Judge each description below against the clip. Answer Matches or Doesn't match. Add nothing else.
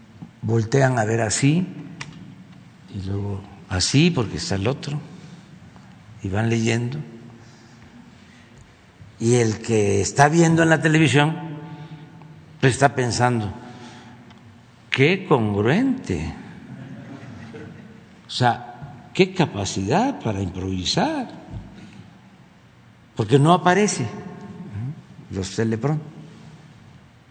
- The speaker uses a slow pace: Matches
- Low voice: Matches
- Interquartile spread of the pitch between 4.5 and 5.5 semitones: Matches